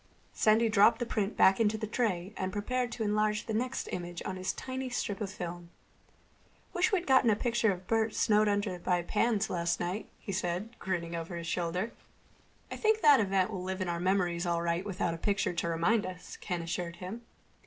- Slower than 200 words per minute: No, fast, 205 wpm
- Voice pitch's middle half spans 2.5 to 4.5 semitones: Yes, average, 4.0 semitones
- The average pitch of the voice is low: No, high, 195 Hz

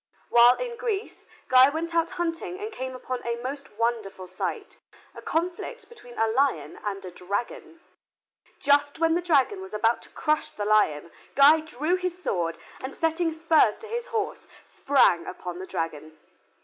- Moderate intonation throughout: No, wide, 7.9 semitones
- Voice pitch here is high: Yes, very high, 280 Hz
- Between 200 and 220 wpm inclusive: No, average, 165 wpm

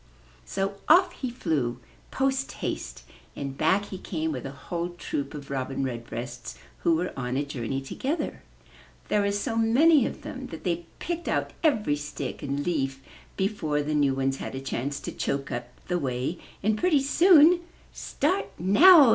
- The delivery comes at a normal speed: Yes, average, 170 wpm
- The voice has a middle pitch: Yes, medium, 165 Hz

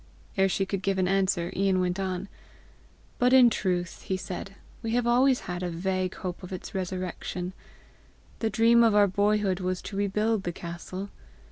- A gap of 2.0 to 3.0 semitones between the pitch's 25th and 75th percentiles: Yes, narrow, 2.4 semitones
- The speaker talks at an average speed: Yes, average, 175 wpm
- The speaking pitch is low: No, high, 190 Hz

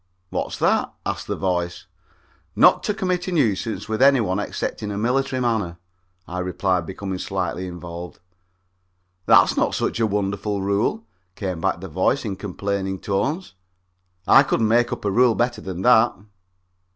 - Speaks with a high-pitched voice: No, low, 100 Hz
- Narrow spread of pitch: No, average, 4.4 semitones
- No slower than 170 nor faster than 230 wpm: No, average, 160 wpm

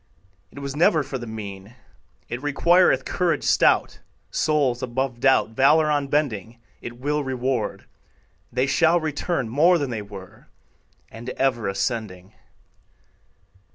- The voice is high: No, low, 130 Hz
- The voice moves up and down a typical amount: Yes, average, 4.3 semitones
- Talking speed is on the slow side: Yes, slow, 120 wpm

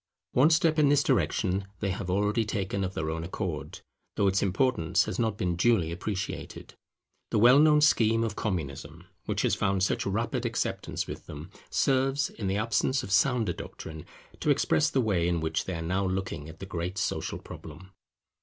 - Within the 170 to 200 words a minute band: Yes, average, 185 wpm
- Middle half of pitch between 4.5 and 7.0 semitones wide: Yes, average, 5.1 semitones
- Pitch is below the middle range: Yes, low, 100 Hz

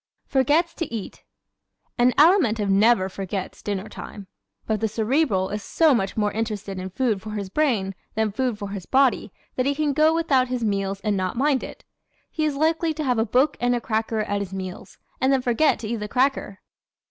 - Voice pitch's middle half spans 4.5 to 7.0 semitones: Yes, average, 5.1 semitones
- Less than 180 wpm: No, fast, 205 wpm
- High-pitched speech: Yes, high, 225 Hz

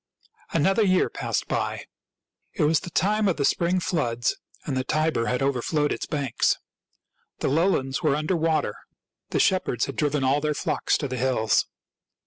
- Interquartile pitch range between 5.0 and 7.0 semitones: No, average, 4.3 semitones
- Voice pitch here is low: No, medium, 150 Hz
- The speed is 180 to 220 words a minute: No, average, 165 wpm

